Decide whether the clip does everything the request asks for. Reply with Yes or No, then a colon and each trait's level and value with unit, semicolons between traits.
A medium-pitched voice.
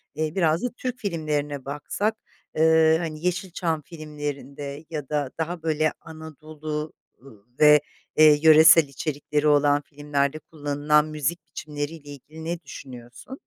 Yes: medium, 155 Hz